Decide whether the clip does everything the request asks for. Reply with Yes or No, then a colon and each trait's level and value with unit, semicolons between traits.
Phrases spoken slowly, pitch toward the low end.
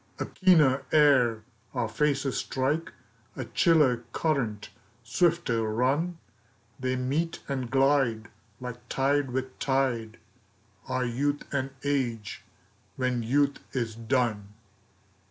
Yes: slow, 105 wpm; low, 130 Hz